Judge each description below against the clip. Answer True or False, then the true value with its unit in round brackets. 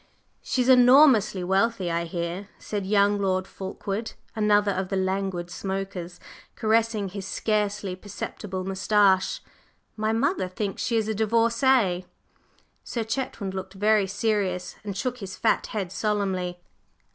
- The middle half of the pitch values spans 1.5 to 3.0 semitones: True (2.6 semitones)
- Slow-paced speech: True (130 wpm)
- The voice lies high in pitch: True (200 Hz)